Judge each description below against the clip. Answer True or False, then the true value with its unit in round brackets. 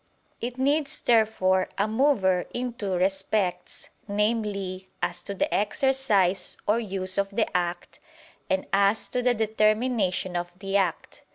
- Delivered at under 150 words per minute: True (135 wpm)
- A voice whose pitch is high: True (200 Hz)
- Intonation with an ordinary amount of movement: True (3.7 semitones)